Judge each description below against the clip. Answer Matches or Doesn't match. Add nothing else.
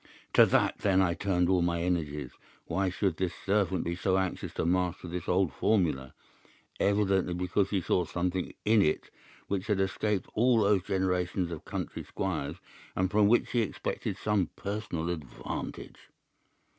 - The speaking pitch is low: Matches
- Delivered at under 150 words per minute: Doesn't match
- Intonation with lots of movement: Doesn't match